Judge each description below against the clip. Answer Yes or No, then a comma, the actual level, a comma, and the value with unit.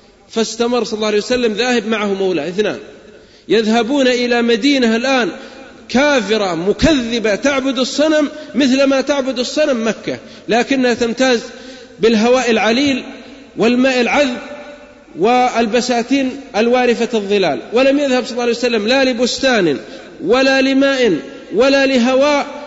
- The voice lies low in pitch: No, very high, 250 Hz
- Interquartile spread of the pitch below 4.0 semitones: Yes, average, 2.7 semitones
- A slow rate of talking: Yes, slow, 115 wpm